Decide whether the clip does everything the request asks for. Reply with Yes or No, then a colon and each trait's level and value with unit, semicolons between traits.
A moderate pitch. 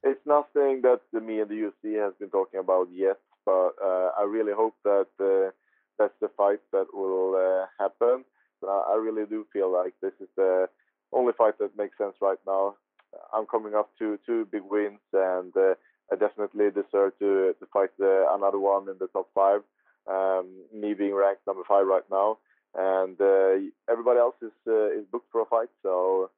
No: low, 100 Hz